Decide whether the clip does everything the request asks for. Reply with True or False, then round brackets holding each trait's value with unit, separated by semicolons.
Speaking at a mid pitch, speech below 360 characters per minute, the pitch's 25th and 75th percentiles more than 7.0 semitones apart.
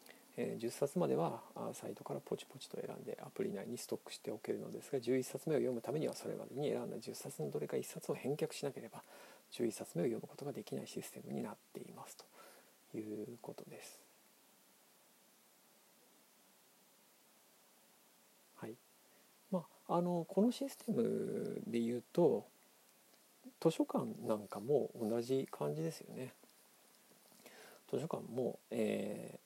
True (180 Hz; 225 characters per minute; 8.8 semitones)